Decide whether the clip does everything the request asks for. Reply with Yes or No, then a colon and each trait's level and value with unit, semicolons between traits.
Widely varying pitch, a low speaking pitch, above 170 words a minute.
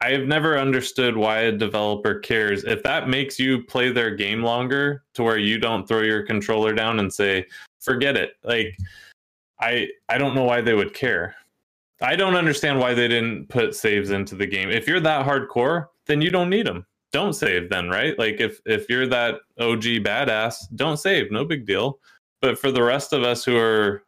No: average, 3.7 semitones; low, 120 Hz; average, 200 wpm